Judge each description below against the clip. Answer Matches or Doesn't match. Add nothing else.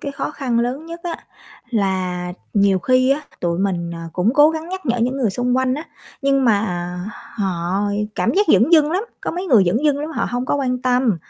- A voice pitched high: Matches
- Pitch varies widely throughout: Matches